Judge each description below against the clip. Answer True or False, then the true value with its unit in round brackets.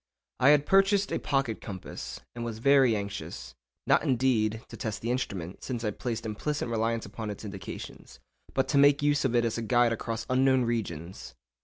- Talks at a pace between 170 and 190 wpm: True (175 wpm)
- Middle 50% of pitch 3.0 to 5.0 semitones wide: True (3.8 semitones)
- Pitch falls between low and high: False (115 Hz)